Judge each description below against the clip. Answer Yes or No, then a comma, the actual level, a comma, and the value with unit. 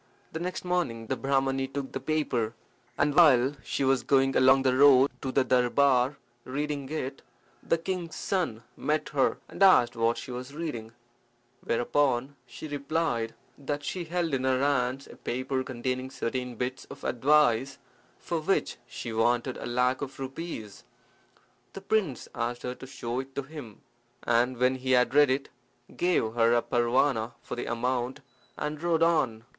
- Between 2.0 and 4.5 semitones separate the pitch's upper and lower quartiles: Yes, average, 3.1 semitones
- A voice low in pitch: Yes, low, 130 Hz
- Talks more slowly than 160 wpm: No, average, 165 wpm